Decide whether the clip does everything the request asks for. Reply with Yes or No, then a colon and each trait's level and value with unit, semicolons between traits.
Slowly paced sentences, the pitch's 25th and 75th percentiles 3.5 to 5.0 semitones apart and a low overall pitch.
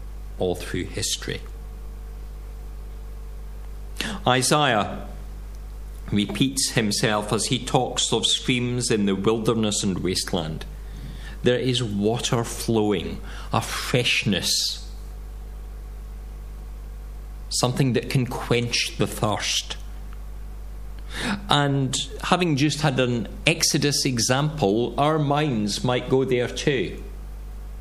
Yes: slow, 90 wpm; average, 4.5 semitones; low, 120 Hz